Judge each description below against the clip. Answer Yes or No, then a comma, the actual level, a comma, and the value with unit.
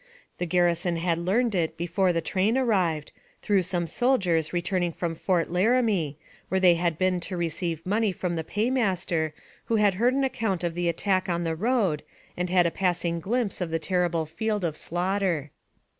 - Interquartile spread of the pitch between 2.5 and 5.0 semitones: Yes, average, 3.2 semitones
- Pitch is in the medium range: Yes, medium, 180 Hz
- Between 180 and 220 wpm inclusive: Yes, average, 185 wpm